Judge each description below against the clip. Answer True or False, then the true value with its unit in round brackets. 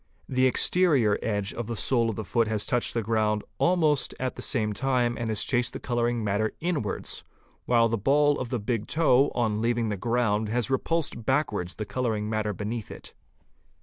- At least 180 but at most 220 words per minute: True (190 wpm)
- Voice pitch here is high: False (115 Hz)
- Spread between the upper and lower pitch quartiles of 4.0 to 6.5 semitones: False (3.2 semitones)